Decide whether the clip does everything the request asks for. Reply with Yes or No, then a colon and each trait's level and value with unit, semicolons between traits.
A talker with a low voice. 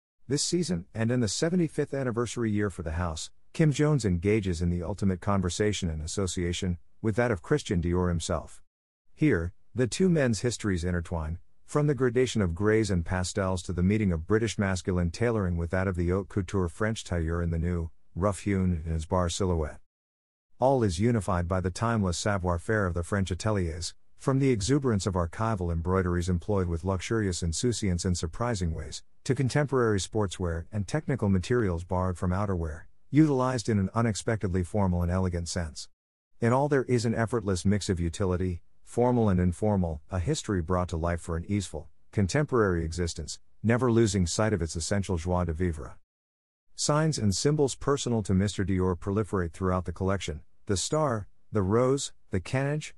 Yes: very low, 95 Hz